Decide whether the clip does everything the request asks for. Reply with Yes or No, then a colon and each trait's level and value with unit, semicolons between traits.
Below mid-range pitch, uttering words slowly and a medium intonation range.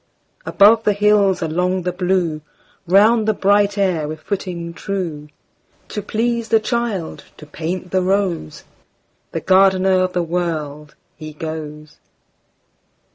No: medium, 185 Hz; slow, 115 wpm; average, 3.9 semitones